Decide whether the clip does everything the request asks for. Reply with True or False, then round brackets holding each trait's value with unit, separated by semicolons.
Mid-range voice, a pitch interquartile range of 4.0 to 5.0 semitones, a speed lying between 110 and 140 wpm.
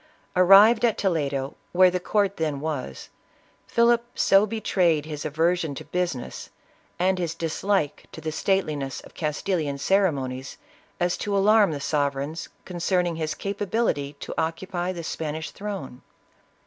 True (170 Hz; 4.5 semitones; 135 wpm)